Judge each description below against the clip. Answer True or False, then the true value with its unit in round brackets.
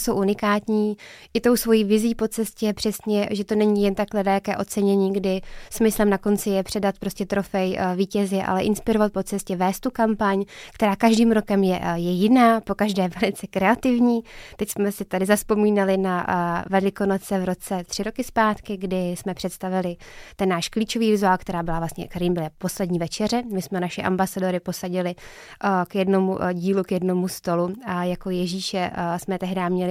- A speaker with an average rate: False (175 wpm)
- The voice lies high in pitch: True (195 Hz)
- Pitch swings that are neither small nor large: False (2.3 semitones)